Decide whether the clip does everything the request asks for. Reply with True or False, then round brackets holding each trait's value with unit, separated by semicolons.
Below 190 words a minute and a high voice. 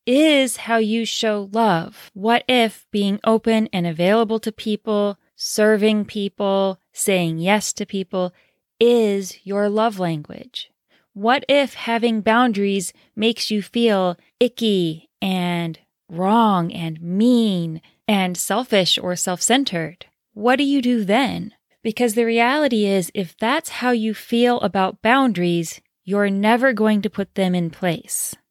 True (135 wpm; 210 Hz)